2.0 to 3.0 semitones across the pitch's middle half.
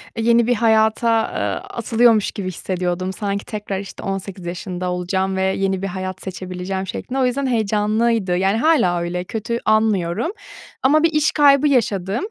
No: average, 3.8 semitones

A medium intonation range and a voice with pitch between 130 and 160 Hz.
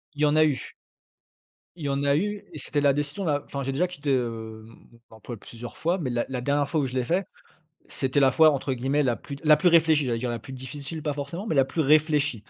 Yes: average, 3.1 semitones; medium, 140 Hz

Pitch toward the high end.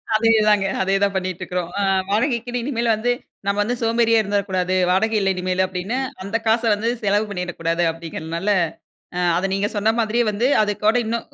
Yes: high, 205 Hz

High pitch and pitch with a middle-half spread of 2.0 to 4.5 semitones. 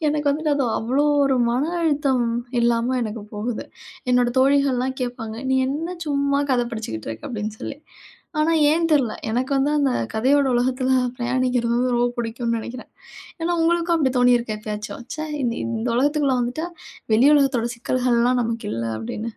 Yes: very high, 250 Hz; average, 3.3 semitones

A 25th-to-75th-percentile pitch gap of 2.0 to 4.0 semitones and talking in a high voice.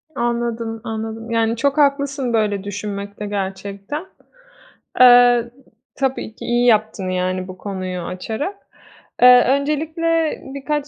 No: average, 5.2 semitones; high, 230 Hz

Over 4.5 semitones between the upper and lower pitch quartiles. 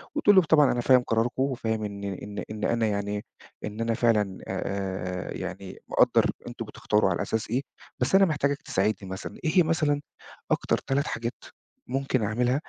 Yes: average, 5.0 semitones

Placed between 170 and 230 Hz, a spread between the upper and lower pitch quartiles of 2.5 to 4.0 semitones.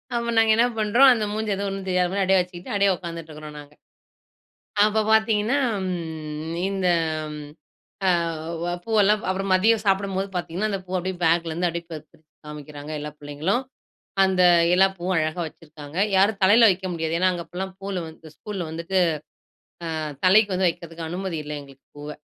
Yes: medium, 185 Hz; average, 3.5 semitones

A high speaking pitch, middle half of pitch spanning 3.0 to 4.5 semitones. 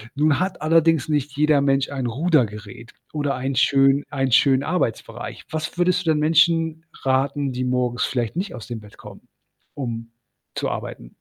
No: medium, 140 Hz; average, 3.6 semitones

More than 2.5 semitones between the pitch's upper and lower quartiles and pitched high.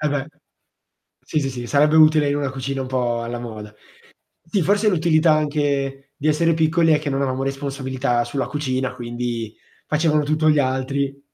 No: average, 2.9 semitones; medium, 140 Hz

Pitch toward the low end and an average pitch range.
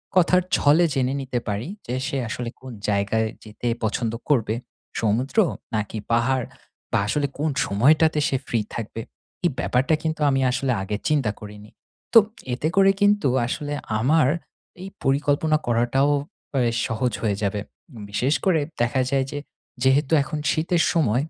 Yes: low, 130 Hz; average, 4.9 semitones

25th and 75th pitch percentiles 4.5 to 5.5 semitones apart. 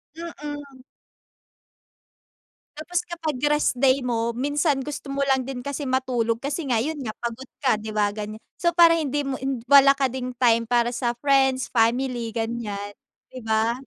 No: average, 3.3 semitones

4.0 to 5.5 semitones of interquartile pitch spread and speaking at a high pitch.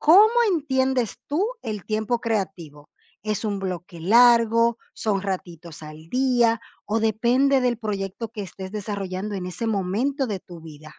Yes: average, 4.3 semitones; high, 215 Hz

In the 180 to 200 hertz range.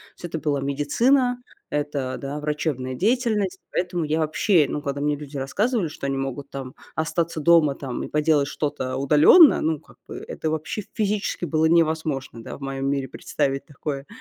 No: medium, 150 Hz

